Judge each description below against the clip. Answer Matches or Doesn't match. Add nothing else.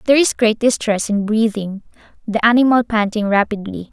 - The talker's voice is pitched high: Matches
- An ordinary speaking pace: Matches